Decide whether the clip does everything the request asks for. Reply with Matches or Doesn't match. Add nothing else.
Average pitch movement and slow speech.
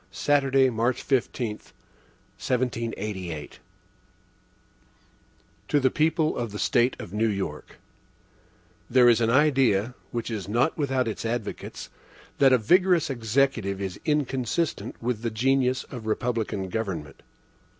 Matches